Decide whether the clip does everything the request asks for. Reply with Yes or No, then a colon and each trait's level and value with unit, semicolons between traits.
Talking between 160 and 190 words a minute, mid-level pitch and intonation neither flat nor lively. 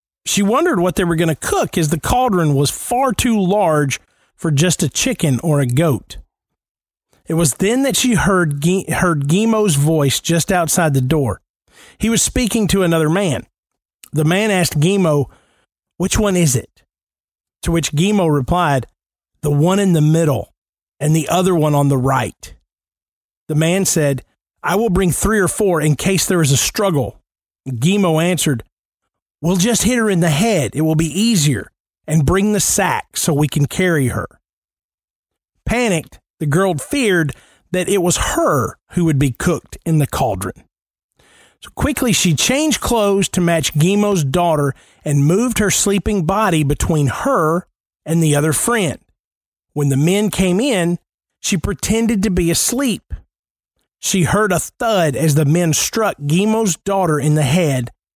Yes: average, 165 wpm; medium, 165 Hz; average, 5.0 semitones